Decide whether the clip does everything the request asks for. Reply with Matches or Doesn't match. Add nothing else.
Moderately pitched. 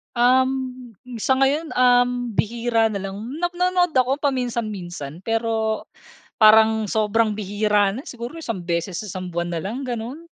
Doesn't match